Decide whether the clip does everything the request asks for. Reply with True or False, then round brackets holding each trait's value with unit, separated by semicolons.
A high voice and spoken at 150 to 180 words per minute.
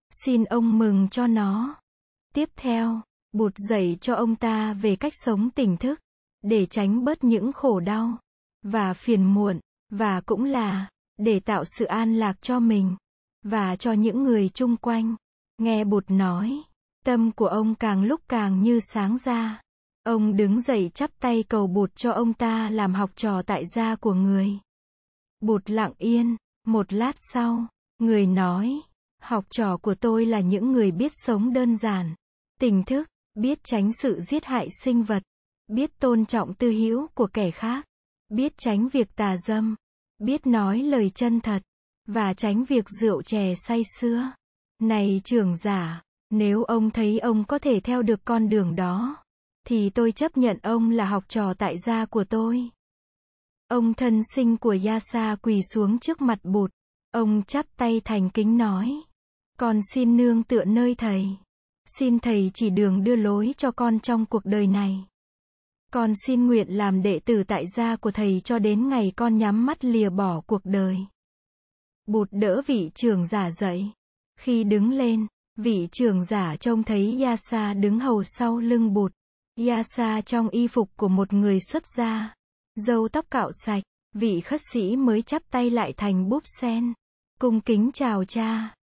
True (225 Hz; 170 wpm)